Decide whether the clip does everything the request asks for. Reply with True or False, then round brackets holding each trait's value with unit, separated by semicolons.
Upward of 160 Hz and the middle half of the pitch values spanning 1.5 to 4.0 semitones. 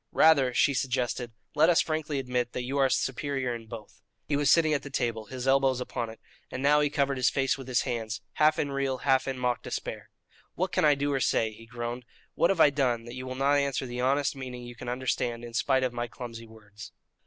False (130 Hz; 2.6 semitones)